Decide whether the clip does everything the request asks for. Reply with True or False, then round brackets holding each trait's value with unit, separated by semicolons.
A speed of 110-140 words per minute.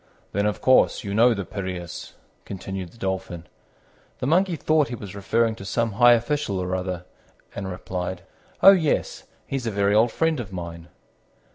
False (170 wpm)